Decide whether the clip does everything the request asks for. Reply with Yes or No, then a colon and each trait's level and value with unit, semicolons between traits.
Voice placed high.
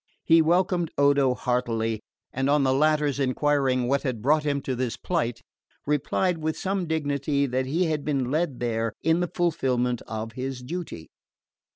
No: medium, 140 Hz